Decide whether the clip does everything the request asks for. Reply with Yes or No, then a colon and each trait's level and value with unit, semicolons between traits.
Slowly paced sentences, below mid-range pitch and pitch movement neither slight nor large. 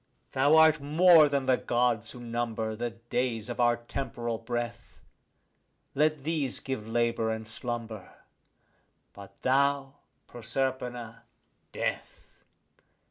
Yes: slow, 110 wpm; low, 120 Hz; average, 3.0 semitones